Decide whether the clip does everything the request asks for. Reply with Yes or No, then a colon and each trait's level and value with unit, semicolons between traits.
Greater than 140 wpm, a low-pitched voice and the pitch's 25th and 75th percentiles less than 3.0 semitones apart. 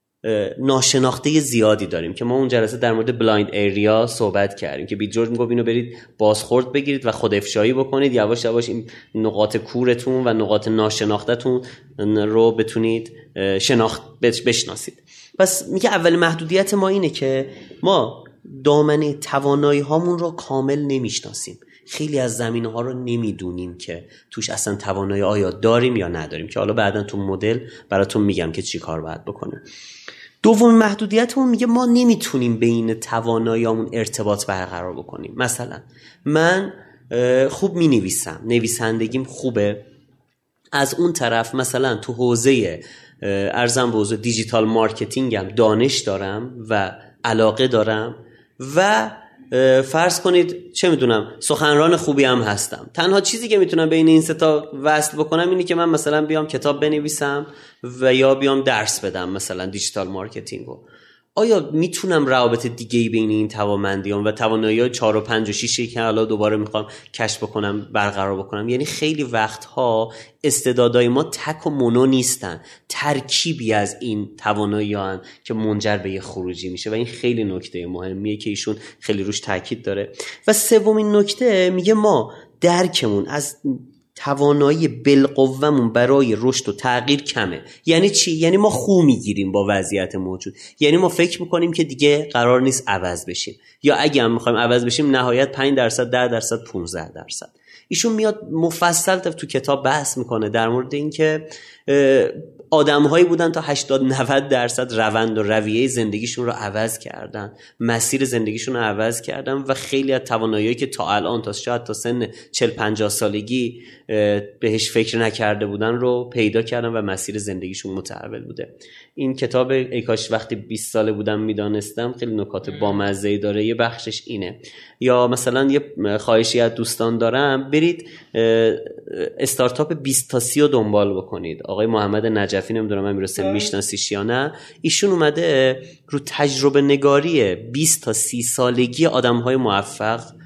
No: average, 150 wpm; low, 120 Hz; average, 4.9 semitones